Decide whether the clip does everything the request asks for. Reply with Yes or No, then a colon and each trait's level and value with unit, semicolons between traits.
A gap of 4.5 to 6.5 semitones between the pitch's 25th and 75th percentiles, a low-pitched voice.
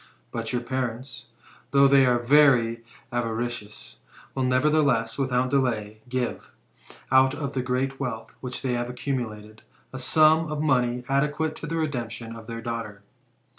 No: average, 3.0 semitones; low, 125 Hz